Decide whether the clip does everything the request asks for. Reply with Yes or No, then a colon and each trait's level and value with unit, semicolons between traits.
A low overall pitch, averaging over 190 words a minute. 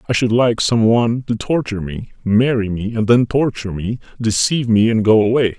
Yes: low, 115 Hz; fast, 205 wpm